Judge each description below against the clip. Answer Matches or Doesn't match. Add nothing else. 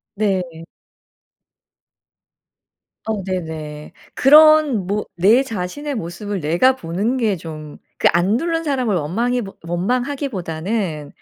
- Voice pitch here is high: Matches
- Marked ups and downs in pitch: Matches